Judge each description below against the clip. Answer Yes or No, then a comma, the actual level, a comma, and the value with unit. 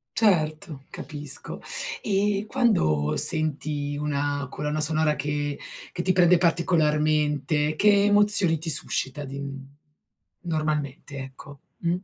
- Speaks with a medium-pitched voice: Yes, medium, 155 Hz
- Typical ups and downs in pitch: Yes, average, 3.3 semitones